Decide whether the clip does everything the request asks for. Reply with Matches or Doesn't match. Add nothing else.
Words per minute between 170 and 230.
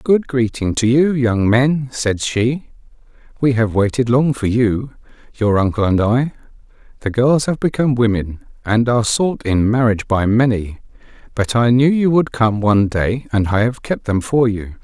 Matches